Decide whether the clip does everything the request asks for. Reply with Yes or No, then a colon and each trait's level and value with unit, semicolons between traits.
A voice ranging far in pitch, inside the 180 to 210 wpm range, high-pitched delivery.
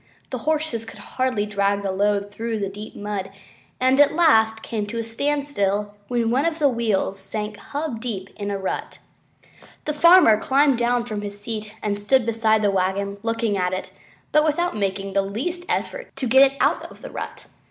No: average, 4.7 semitones; average, 195 wpm; high, 220 Hz